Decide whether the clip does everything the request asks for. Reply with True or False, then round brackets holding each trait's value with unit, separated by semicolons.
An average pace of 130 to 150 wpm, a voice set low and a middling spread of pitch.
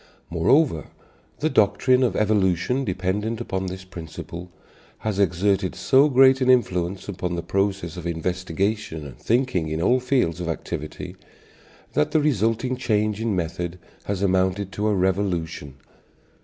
True (140 wpm; 95 Hz; 4.3 semitones)